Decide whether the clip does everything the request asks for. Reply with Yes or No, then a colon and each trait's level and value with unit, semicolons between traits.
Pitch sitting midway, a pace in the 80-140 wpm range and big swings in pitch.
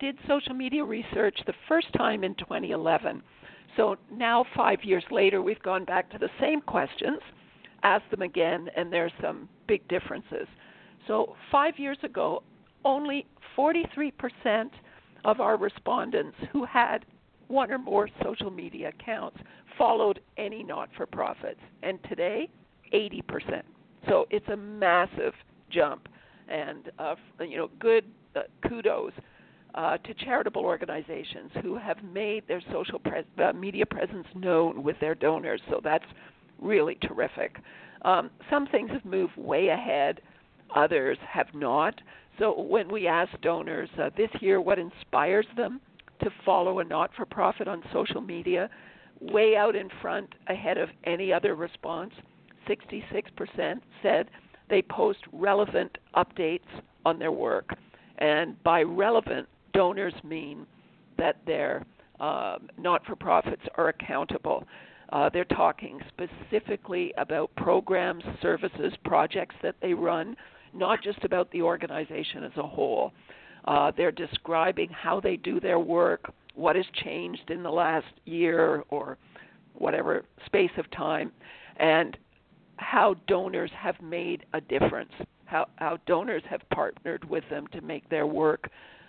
No: high, 210 Hz; slow, 135 wpm; wide, 7.9 semitones